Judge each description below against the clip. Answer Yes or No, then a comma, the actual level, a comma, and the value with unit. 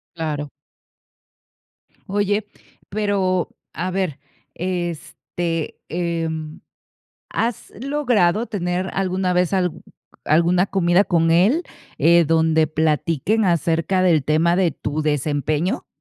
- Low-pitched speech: No, medium, 175 Hz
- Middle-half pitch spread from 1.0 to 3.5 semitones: Yes, average, 2.9 semitones